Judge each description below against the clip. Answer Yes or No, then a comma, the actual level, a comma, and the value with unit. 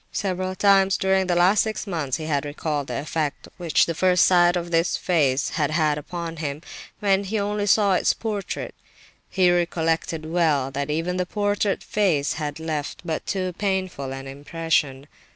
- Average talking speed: Yes, average, 170 wpm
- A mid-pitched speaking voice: Yes, medium, 170 Hz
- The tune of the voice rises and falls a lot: No, average, 4.1 semitones